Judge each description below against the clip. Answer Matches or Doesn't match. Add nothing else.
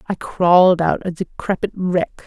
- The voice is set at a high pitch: Doesn't match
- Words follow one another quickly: Doesn't match